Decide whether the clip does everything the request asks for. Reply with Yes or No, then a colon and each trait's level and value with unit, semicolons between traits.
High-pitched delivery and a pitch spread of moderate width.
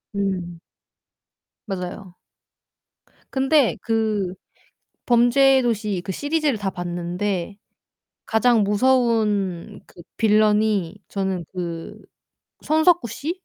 Yes: high, 210 Hz; average, 4.6 semitones